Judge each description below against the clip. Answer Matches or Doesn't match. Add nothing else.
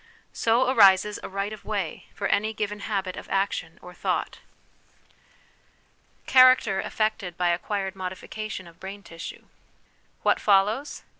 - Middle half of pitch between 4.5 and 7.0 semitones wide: Doesn't match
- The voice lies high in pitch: Matches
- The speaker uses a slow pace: Matches